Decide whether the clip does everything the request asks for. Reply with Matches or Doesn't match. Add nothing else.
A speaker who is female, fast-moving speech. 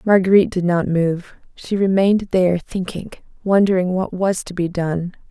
Doesn't match